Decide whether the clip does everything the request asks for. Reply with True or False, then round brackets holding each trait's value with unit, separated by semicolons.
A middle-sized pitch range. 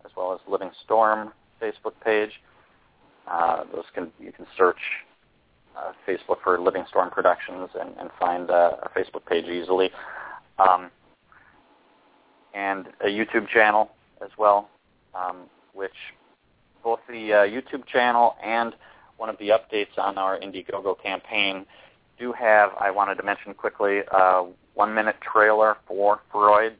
False (2.3 semitones)